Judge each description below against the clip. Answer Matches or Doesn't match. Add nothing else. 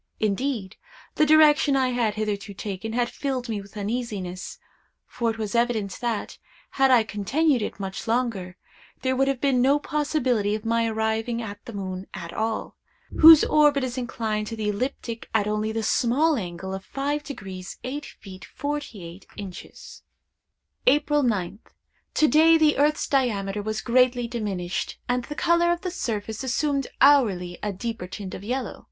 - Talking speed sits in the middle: Matches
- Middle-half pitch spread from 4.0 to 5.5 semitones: Matches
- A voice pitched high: Matches